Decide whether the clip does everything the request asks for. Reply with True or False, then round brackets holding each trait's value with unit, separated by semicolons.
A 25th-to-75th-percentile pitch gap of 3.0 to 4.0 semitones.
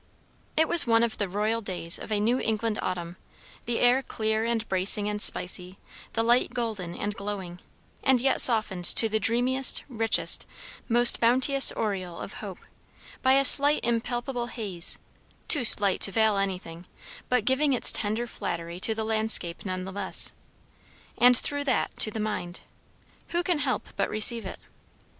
True (3.6 semitones)